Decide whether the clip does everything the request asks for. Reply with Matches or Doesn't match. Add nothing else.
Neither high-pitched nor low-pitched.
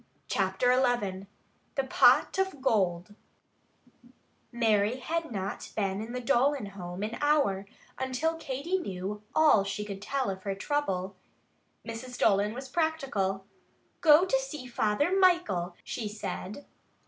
Doesn't match